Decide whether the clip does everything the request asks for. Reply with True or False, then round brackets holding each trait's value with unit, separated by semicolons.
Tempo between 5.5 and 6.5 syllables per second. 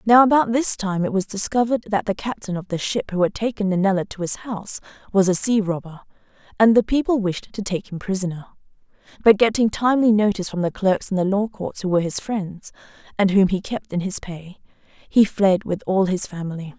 True (5.6 syllables/s)